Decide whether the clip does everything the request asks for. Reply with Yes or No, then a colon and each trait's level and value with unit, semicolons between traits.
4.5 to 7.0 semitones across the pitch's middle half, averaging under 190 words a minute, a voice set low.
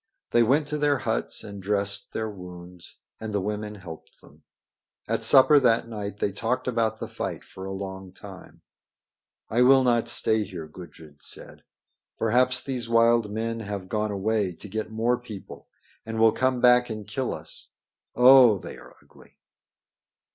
No: average, 3.5 semitones; average, 165 wpm; low, 110 Hz